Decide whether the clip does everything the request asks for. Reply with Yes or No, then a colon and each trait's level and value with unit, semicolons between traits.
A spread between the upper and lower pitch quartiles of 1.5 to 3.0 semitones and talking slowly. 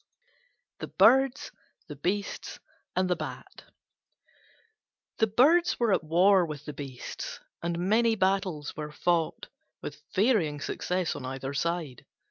No: average, 5.3 semitones; slow, 125 wpm